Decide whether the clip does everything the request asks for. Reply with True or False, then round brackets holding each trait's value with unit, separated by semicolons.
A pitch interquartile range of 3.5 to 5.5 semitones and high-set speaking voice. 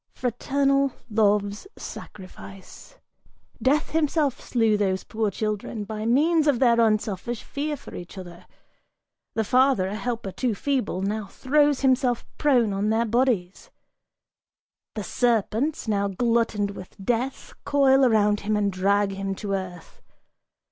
True (4.6 semitones; 220 Hz)